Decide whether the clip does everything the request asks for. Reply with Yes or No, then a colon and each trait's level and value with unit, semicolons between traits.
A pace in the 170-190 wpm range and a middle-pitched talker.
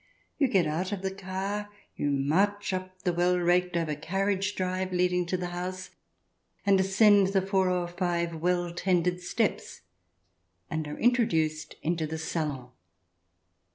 No: average, 150 wpm; medium, 180 Hz